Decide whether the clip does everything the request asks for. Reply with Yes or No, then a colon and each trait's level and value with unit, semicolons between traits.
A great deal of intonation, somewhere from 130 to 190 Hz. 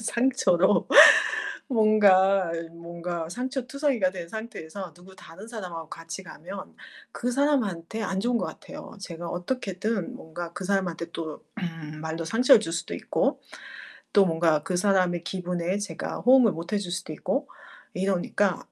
No: average, 4.4 semitones; medium, 185 Hz